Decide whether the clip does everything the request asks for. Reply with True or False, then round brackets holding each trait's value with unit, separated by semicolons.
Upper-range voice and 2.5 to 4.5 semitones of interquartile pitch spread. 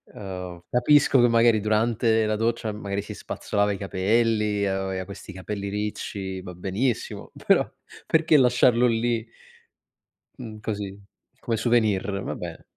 False (105 Hz; 2.9 semitones)